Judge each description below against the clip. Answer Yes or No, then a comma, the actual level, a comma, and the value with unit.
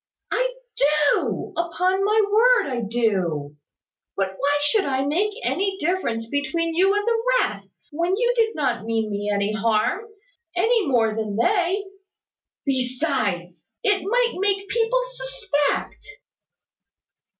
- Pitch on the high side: Yes, very high, 325 Hz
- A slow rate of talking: Yes, slow, 130 wpm